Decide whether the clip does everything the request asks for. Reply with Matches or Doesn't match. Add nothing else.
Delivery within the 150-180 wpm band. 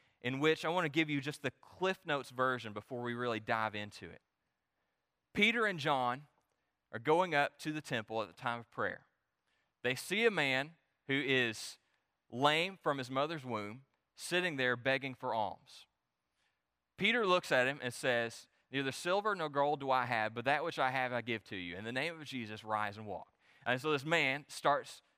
Doesn't match